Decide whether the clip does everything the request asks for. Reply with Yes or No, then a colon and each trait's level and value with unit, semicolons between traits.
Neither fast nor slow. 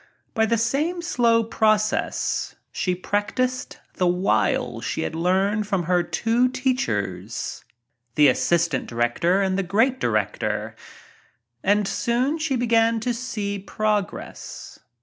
No: slow, 130 wpm